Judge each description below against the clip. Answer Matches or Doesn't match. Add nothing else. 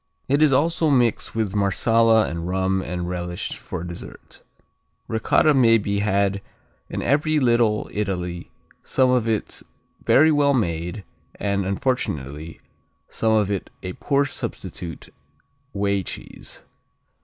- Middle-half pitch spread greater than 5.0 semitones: Matches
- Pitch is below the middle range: Matches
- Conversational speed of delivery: Doesn't match